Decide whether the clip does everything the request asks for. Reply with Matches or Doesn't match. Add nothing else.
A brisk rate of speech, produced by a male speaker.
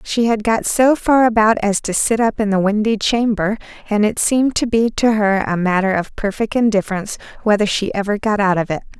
Doesn't match